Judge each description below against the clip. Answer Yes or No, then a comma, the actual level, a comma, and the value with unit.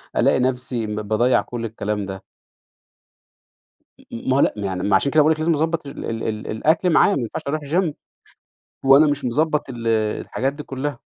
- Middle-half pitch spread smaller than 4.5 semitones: No, average, 5.2 semitones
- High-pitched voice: No, low, 130 Hz